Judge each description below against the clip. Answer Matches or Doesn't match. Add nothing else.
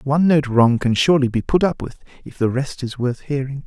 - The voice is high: Doesn't match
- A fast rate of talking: Matches